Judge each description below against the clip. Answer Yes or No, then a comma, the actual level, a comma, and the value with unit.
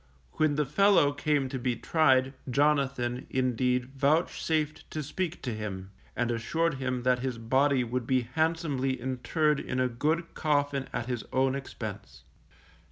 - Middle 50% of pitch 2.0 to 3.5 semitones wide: Yes, average, 3.2 semitones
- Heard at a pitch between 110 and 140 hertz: Yes, low, 135 Hz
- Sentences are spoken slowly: No, average, 150 wpm